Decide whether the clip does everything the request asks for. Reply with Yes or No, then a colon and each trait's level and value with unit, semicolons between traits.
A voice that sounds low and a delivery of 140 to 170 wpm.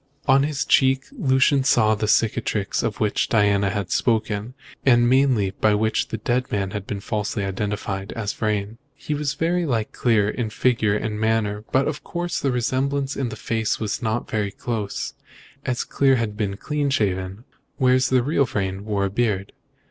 No: low, 110 Hz; average, 180 wpm